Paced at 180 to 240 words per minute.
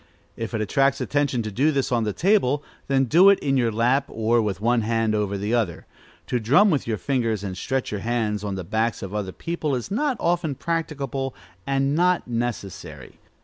Yes: fast, 205 wpm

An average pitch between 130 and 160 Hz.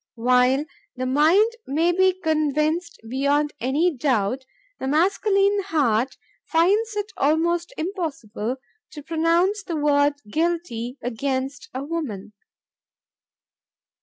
No: very high, 300 Hz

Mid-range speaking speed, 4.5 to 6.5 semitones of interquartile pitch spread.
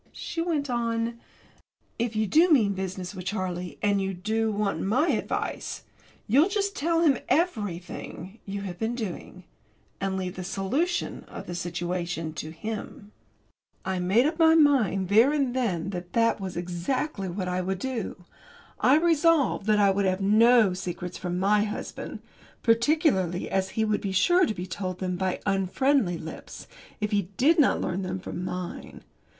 Yes: average, 165 wpm; average, 5.2 semitones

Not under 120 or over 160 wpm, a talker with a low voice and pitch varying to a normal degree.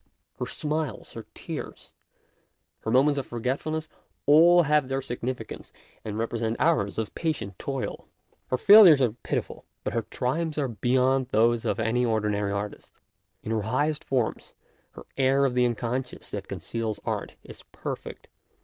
Yes: average, 150 wpm; low, 125 Hz; average, 4.4 semitones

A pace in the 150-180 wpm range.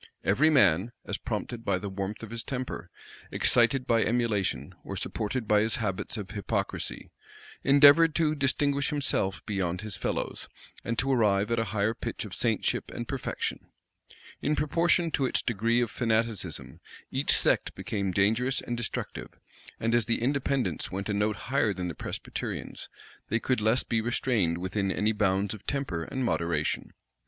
Yes: average, 165 wpm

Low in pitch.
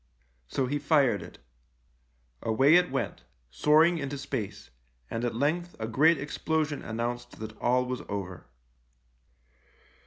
Yes: low, 130 Hz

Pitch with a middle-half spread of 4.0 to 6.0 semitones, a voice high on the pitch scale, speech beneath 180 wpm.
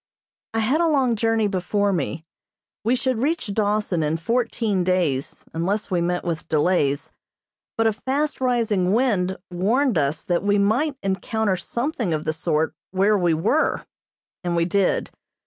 Yes: average, 5.0 semitones; high, 200 Hz; average, 155 wpm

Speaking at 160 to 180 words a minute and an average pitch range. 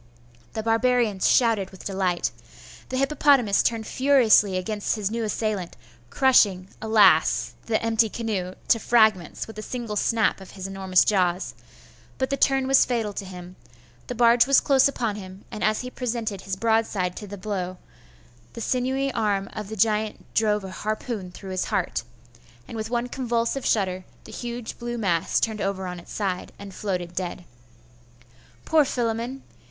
Yes: average, 165 wpm; average, 3.7 semitones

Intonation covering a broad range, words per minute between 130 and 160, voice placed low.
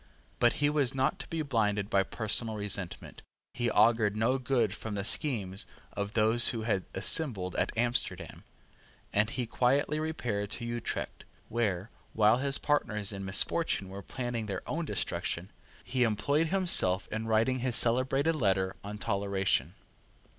No: average, 4.3 semitones; average, 150 wpm; low, 110 Hz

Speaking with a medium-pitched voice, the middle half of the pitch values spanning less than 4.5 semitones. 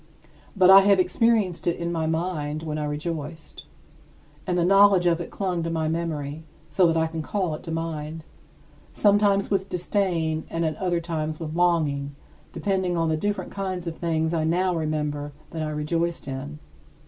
Yes: medium, 165 Hz; average, 2.7 semitones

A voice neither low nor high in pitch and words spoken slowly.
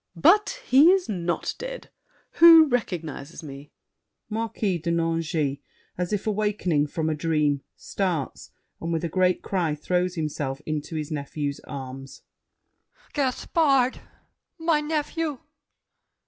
Yes: medium, 175 Hz; slow, 120 wpm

